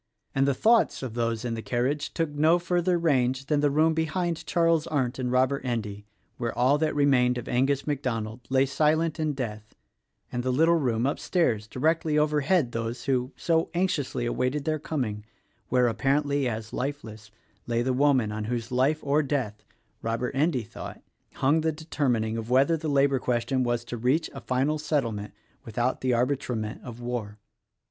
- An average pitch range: Yes, average, 4.0 semitones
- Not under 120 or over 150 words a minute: No, average, 180 wpm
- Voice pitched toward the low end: Yes, low, 130 Hz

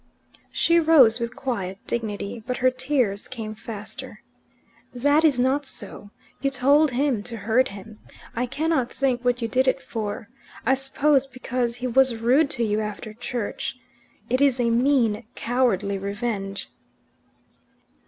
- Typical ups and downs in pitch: Yes, average, 3.5 semitones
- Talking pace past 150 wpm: No, average, 145 wpm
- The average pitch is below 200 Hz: No, high, 245 Hz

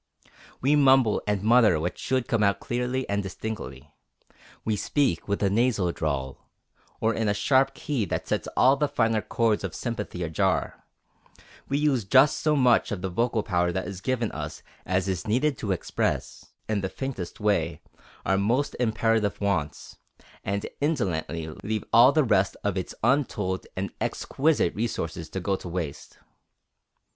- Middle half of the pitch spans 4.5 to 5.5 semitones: Yes, average, 5.2 semitones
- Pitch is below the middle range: Yes, low, 105 Hz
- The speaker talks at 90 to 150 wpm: No, average, 160 wpm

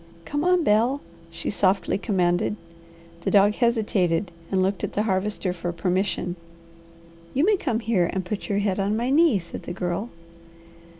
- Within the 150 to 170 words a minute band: Yes, average, 165 wpm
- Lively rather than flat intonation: No, average, 3.9 semitones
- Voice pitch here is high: Yes, high, 200 Hz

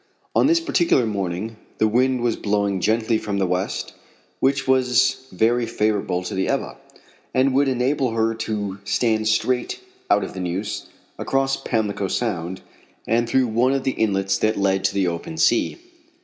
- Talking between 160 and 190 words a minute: Yes, average, 165 wpm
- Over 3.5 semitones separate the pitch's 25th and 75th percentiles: Yes, average, 4.5 semitones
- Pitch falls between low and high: No, low, 110 Hz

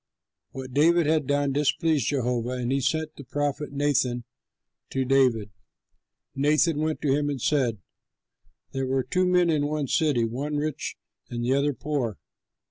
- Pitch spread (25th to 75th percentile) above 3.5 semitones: No, average, 2.8 semitones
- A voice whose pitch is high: No, medium, 140 Hz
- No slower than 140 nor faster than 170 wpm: Yes, average, 160 wpm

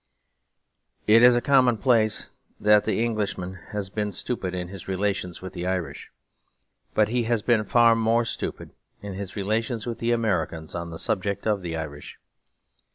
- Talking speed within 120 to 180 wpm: Yes, average, 160 wpm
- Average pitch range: Yes, average, 3.8 semitones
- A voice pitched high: No, low, 105 Hz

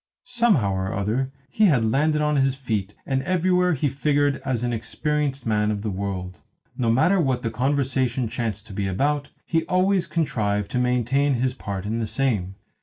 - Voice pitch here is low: Yes, low, 130 Hz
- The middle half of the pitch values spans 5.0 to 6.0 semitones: Yes, wide, 5.5 semitones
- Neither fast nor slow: Yes, average, 180 wpm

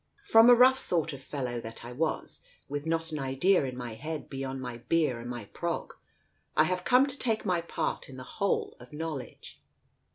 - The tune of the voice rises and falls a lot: Yes, wide, 6.1 semitones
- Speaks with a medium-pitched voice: Yes, medium, 150 Hz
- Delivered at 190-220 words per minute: Yes, average, 200 wpm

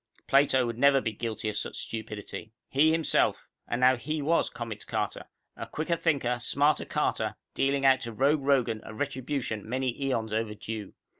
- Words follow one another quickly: No, average, 165 wpm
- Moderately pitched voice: No, low, 125 Hz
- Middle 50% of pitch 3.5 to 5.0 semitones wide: Yes, average, 4.0 semitones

